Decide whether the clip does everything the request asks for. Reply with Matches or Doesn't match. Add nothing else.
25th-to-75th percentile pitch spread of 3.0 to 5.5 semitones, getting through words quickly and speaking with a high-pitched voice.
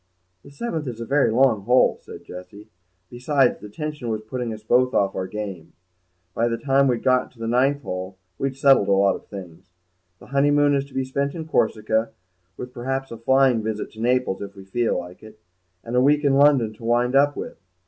Doesn't match